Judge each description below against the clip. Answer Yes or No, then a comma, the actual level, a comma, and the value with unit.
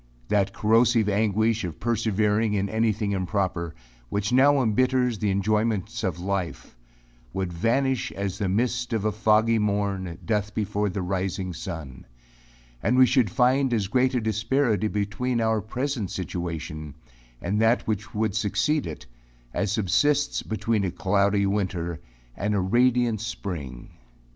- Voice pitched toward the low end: Yes, low, 105 Hz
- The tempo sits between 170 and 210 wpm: No, average, 145 wpm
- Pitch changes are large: No, average, 3.2 semitones